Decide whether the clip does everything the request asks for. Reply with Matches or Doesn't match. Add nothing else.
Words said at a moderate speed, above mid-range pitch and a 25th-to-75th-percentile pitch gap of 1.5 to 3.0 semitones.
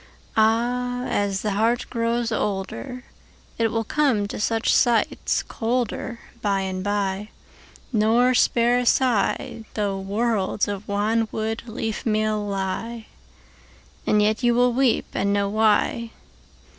Doesn't match